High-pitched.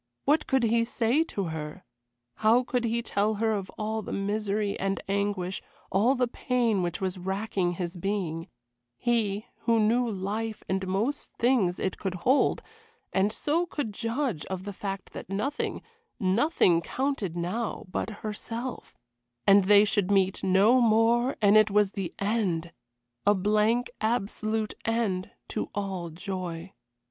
Yes: high, 205 Hz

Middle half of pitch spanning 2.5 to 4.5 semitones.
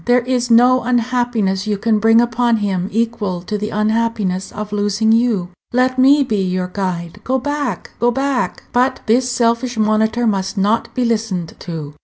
Yes: average, 3.3 semitones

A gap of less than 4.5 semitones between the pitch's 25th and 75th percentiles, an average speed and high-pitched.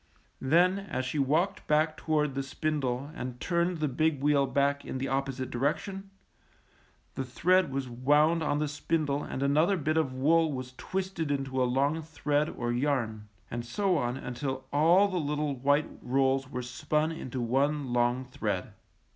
No: average, 3.2 semitones; average, 170 wpm; medium, 140 Hz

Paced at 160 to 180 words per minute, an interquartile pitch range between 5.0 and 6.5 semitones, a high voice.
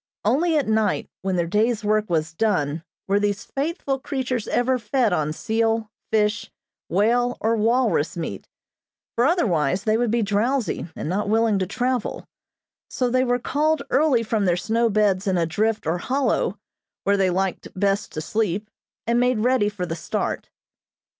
No: average, 165 wpm; average, 4.1 semitones; high, 215 Hz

